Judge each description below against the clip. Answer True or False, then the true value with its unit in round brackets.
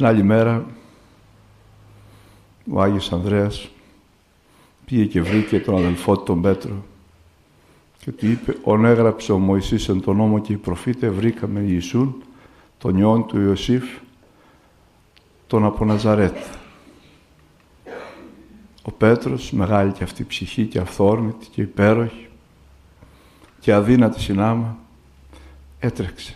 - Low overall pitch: True (105 Hz)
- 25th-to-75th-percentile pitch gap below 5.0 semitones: True (3.2 semitones)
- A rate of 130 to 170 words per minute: False (115 wpm)